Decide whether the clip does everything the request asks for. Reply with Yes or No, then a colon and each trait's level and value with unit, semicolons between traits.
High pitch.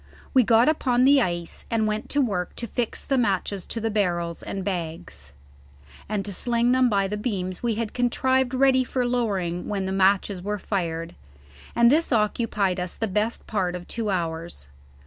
Yes: high, 210 Hz